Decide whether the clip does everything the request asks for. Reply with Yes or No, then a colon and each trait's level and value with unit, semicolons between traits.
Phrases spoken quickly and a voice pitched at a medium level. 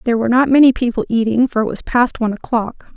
No: fast, 245 wpm; high, 240 Hz